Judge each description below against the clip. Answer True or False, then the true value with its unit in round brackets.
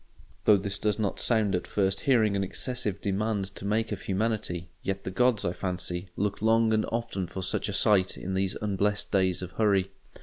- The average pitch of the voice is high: False (100 Hz)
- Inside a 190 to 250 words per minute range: True (200 wpm)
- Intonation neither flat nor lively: False (2.3 semitones)